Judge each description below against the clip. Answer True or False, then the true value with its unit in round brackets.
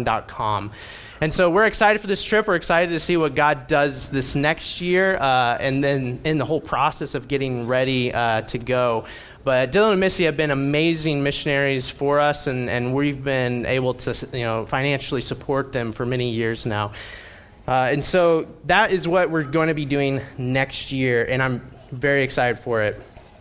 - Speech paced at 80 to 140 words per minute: False (190 wpm)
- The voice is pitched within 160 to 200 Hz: False (135 Hz)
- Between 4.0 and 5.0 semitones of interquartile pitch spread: False (3.6 semitones)